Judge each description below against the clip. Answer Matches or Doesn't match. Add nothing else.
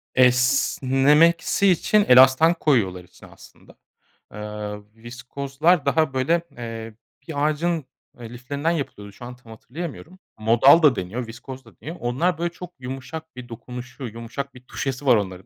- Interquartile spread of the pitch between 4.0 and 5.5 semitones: Matches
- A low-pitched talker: Matches